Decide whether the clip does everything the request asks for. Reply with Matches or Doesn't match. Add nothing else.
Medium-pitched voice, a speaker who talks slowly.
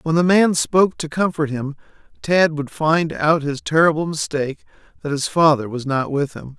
Doesn't match